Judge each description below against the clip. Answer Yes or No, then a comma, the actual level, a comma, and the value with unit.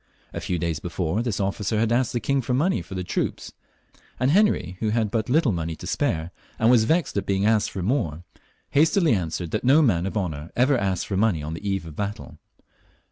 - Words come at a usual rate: No, fast, 225 wpm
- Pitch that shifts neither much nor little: No, wide, 5.8 semitones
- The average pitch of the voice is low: Yes, low, 105 Hz